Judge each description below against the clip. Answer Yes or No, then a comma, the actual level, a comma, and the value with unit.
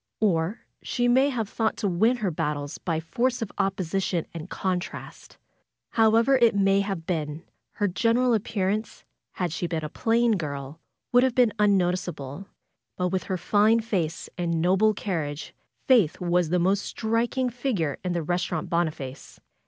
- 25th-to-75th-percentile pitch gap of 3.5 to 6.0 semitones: Yes, average, 5.1 semitones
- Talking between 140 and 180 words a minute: Yes, average, 160 wpm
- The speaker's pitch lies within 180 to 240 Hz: Yes, high, 190 Hz